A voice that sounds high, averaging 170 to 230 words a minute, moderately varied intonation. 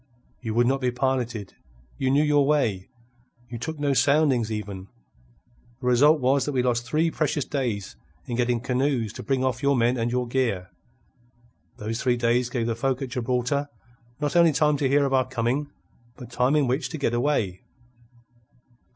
No: low, 125 Hz; average, 180 wpm; average, 3.0 semitones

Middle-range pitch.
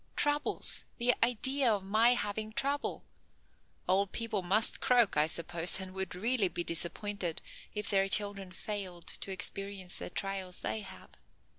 No: high, 200 Hz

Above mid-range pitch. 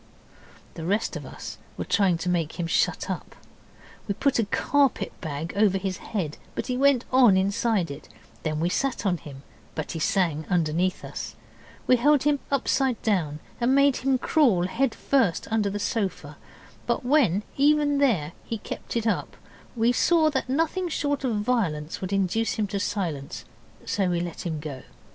Yes: high, 205 Hz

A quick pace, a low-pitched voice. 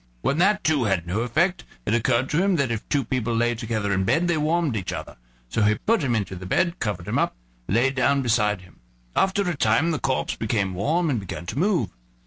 Yes: fast, 235 wpm; low, 120 Hz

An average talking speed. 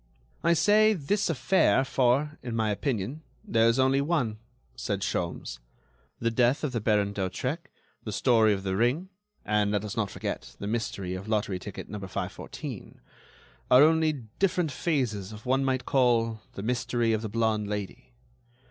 Yes: average, 165 wpm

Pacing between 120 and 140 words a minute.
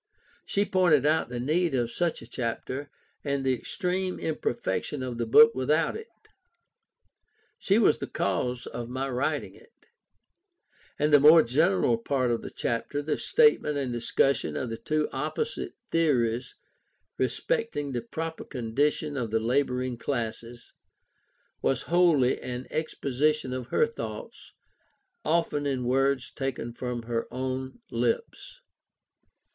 Yes: slow, 135 wpm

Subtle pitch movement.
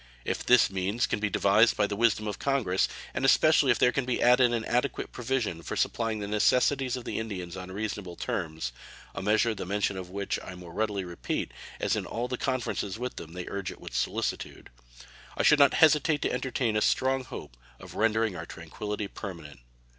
No: average, 4.8 semitones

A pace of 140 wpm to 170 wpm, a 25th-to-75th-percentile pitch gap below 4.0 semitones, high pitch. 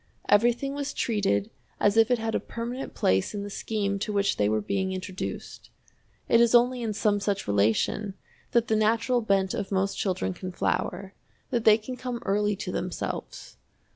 No: average, 180 wpm; average, 3.4 semitones; high, 205 Hz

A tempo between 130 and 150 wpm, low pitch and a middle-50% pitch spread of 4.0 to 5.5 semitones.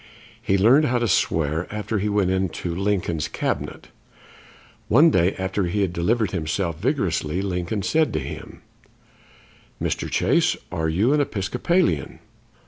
Yes: slow, 135 wpm; very low, 95 Hz; average, 4.6 semitones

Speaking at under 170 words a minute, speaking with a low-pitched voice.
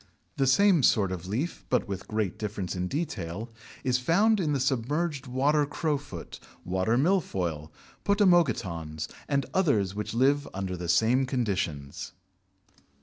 Yes: slow, 135 wpm; low, 120 Hz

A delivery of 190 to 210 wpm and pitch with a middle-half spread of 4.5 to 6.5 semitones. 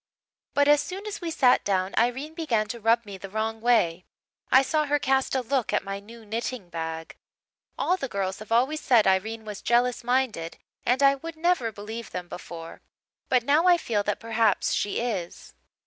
Yes: average, 195 wpm; average, 4.9 semitones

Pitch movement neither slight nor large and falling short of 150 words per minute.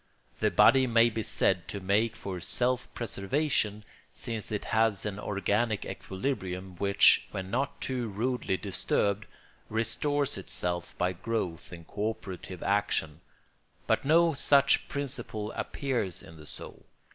Yes: average, 4.3 semitones; slow, 135 wpm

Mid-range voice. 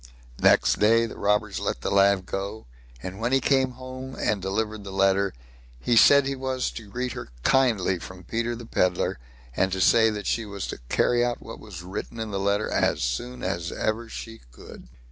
No: low, 110 Hz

